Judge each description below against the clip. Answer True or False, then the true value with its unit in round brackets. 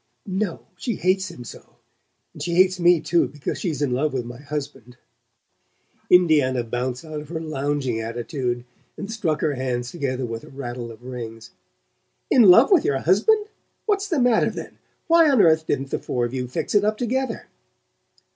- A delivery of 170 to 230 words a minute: True (180 wpm)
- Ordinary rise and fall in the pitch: False (7.1 semitones)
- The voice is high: False (150 Hz)